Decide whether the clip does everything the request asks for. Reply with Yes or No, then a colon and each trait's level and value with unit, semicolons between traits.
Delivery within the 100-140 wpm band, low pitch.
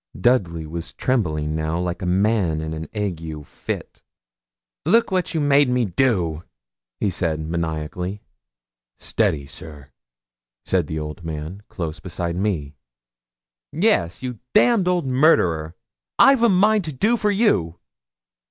Yes: slow, 135 wpm; very low, 90 Hz